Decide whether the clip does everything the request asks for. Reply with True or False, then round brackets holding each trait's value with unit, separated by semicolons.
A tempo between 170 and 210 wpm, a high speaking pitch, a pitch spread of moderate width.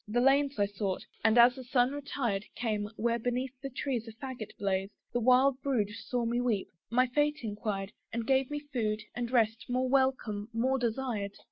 True (190 wpm; 240 Hz; 3.4 semitones)